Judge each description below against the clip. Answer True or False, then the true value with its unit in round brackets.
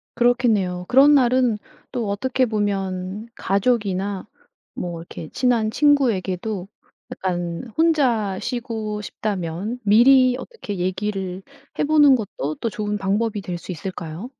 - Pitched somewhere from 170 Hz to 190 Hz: False (210 Hz)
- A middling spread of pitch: True (4.7 semitones)